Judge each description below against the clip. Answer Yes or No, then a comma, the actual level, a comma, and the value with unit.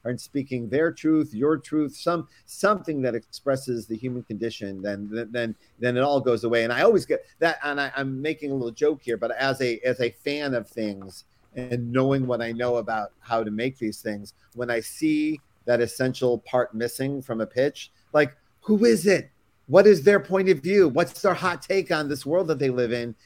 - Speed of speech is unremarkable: No, fast, 215 wpm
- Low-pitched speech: Yes, low, 125 Hz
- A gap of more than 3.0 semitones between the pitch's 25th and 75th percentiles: Yes, average, 5.0 semitones